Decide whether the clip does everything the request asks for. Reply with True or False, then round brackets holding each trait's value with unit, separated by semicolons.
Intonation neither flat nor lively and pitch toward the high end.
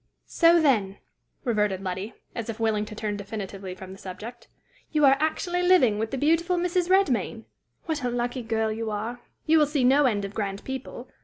False (6.2 semitones; 235 Hz)